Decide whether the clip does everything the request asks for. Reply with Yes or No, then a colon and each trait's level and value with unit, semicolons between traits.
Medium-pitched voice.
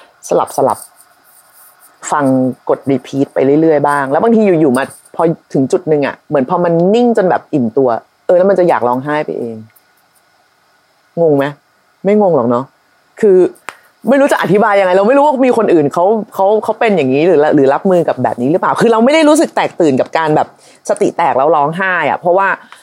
Yes: medium, 175 Hz